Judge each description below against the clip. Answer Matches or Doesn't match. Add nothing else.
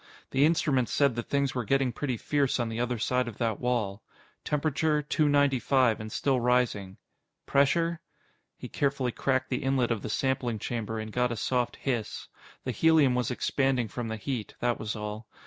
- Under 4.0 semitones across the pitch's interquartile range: Matches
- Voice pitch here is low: Matches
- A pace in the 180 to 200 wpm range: Matches